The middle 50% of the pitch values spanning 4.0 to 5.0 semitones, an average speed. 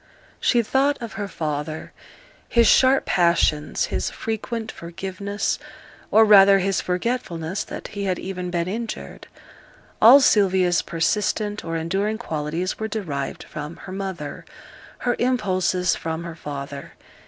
No: average, 4.5 semitones; slow, 130 wpm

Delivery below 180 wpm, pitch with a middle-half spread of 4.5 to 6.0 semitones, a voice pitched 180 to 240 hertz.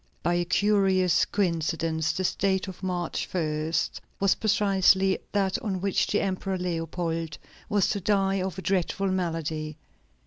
No: average, 140 wpm; average, 2.8 semitones; medium, 185 Hz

